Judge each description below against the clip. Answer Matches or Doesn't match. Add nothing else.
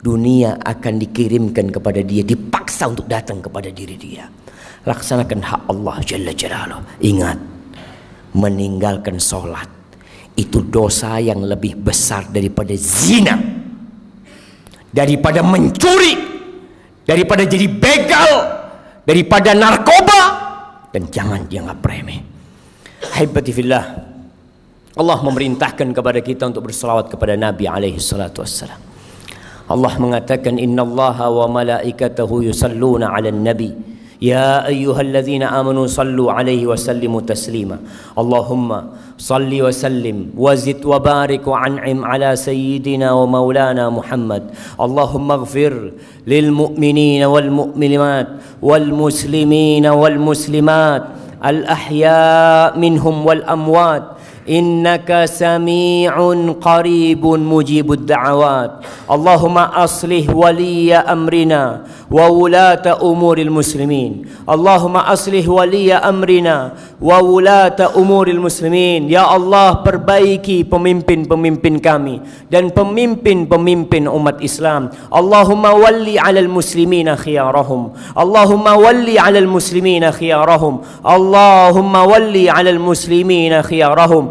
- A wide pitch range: Matches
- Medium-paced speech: Matches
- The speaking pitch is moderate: Matches